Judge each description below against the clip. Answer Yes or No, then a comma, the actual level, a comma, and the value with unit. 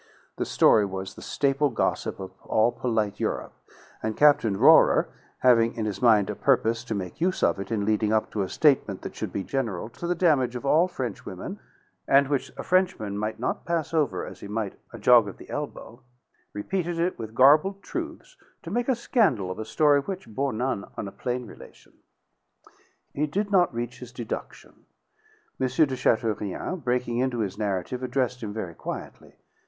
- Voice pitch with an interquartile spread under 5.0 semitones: No, wide, 5.6 semitones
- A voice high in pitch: No, low, 120 Hz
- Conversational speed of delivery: Yes, average, 185 wpm